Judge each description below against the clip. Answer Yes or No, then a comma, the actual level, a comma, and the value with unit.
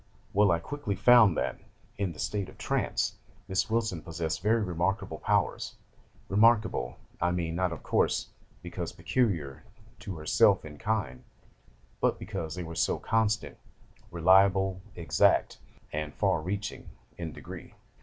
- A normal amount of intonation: Yes, average, 4.2 semitones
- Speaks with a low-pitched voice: Yes, very low, 95 Hz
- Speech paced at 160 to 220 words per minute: No, slow, 135 wpm